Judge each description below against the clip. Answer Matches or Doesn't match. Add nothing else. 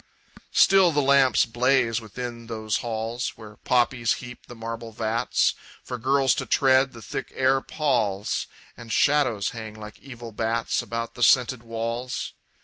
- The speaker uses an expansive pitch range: Doesn't match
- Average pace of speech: Matches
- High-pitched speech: Doesn't match